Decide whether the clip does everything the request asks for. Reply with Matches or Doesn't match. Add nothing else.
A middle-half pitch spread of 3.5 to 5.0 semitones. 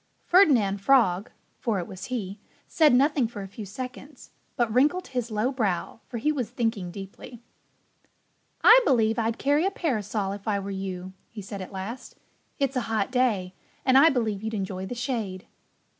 Matches